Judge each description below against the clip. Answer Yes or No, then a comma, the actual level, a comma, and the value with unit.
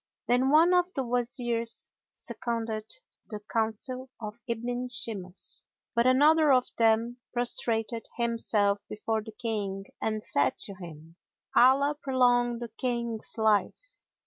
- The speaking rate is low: Yes, slow, 120 wpm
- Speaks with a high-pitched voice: Yes, high, 235 Hz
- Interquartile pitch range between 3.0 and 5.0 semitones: No, narrow, 2.4 semitones